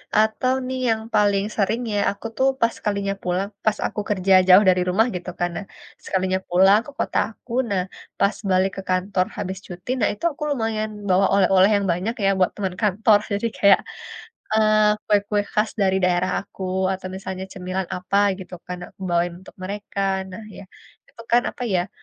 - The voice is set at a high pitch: Yes, high, 200 Hz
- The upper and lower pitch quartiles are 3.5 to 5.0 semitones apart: No, narrow, 2.4 semitones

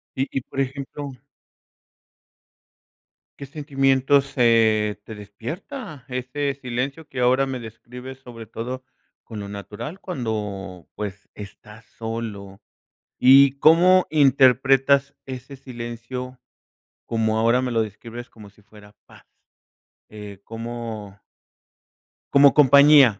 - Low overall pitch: Yes, low, 125 Hz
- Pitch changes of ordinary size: Yes, average, 3.8 semitones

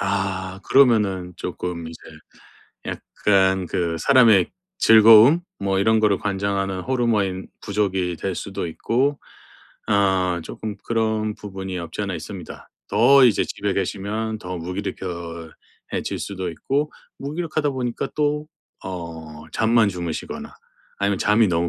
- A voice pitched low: Yes, low, 100 Hz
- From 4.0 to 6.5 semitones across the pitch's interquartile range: No, average, 3.4 semitones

